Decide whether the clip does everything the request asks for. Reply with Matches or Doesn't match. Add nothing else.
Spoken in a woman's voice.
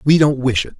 Doesn't match